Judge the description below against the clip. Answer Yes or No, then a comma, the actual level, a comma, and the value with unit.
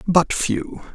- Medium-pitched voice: Yes, medium, 160 Hz